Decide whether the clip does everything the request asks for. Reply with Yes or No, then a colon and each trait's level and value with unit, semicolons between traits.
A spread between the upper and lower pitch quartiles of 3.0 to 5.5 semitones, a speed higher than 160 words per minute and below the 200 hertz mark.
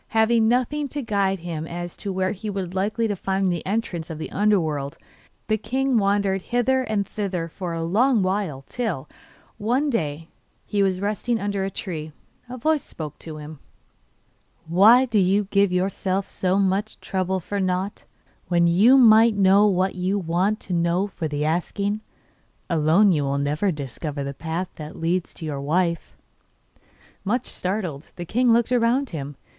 Yes: average, 4.2 semitones; average, 170 wpm; high, 190 Hz